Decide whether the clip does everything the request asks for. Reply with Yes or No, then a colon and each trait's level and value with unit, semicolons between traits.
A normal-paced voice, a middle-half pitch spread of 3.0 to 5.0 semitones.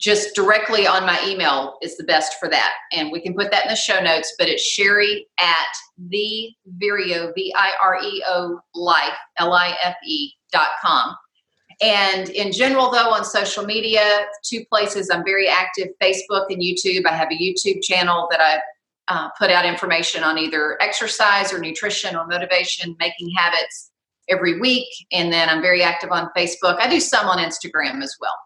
Yes: average, 185 wpm; average, 3.3 semitones